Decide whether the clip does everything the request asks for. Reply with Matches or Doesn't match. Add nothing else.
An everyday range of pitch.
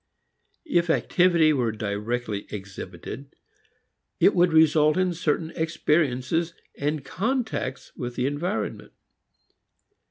Doesn't match